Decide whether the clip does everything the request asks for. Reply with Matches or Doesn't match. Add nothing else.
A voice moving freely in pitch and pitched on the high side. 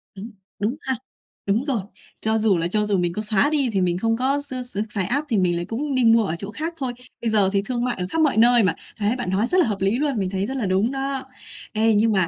Doesn't match